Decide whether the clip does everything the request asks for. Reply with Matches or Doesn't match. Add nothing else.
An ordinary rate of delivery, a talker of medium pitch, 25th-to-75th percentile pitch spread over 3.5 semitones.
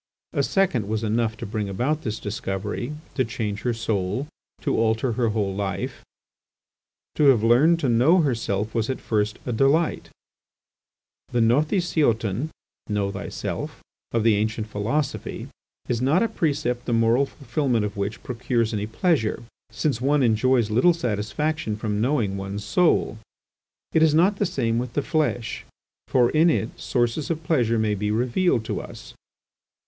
Doesn't match